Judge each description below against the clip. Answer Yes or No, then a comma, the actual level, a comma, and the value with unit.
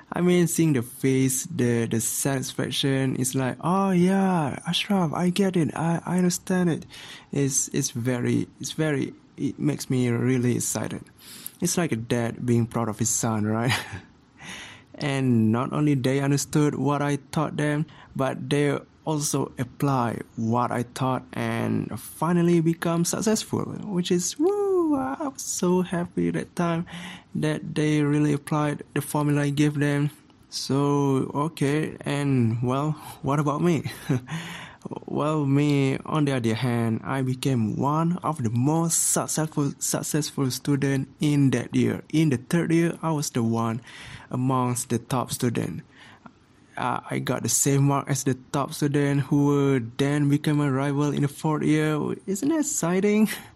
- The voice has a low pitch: No, medium, 145 Hz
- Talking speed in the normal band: Yes, average, 155 wpm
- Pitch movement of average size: Yes, average, 4.0 semitones